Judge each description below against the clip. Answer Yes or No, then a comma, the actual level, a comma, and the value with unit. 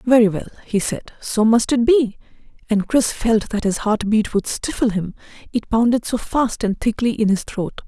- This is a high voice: Yes, high, 225 Hz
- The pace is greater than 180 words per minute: Yes, average, 200 wpm